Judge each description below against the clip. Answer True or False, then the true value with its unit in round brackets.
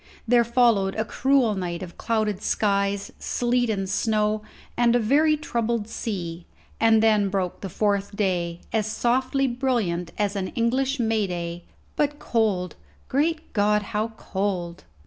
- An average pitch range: True (3.6 semitones)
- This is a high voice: True (215 Hz)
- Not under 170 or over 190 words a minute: False (145 wpm)